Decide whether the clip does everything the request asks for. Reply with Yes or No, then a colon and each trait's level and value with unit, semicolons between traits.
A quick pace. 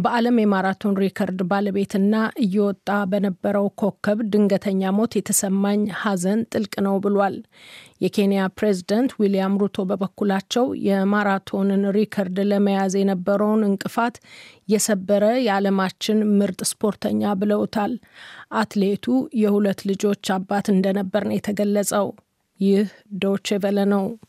No: average, 100 wpm